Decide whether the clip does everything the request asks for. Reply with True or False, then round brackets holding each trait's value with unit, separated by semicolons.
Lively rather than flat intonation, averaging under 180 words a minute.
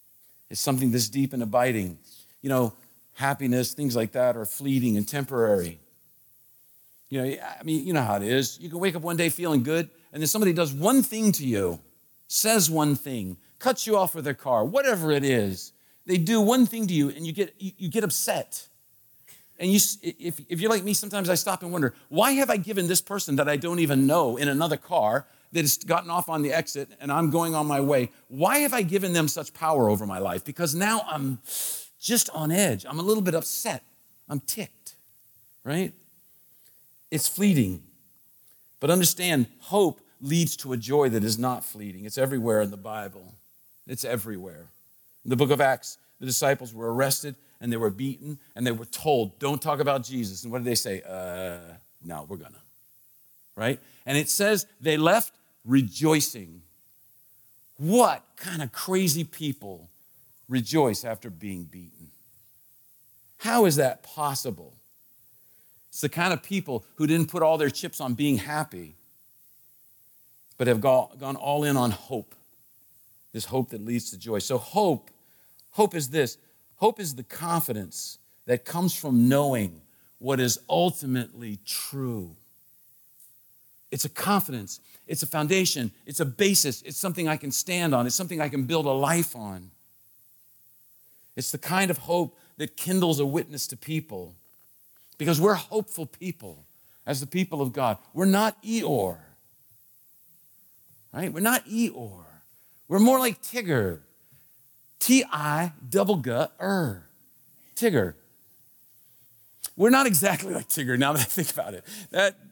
True (6.1 semitones; 165 wpm)